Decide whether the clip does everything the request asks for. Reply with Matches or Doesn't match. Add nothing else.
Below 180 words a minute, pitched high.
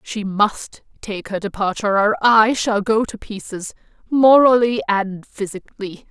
Matches